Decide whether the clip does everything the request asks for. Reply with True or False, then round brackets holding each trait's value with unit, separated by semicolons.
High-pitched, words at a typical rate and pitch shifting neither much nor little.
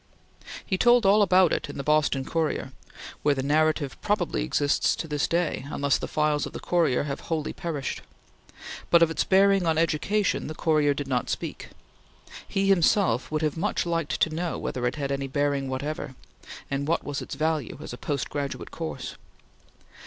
False (155 Hz; 180 wpm; 3.3 semitones)